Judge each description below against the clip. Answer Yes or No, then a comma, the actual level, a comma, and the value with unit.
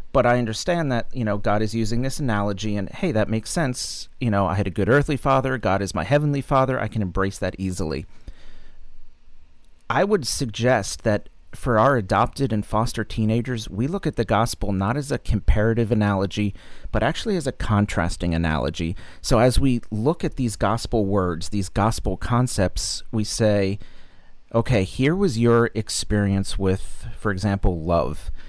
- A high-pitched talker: No, low, 105 Hz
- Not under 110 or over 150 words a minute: No, average, 175 wpm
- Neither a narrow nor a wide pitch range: Yes, average, 4.2 semitones